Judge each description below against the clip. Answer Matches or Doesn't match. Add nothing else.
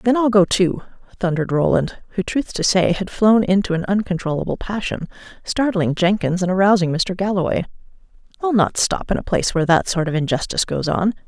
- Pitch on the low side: Doesn't match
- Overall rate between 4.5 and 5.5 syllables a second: Doesn't match